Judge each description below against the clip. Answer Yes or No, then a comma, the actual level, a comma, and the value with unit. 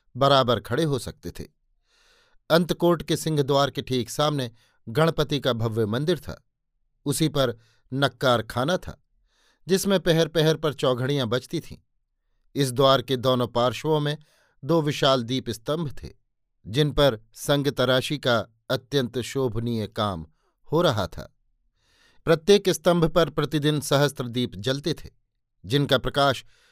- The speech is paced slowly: No, average, 135 wpm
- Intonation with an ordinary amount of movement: Yes, average, 4.1 semitones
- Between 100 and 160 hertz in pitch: Yes, low, 135 Hz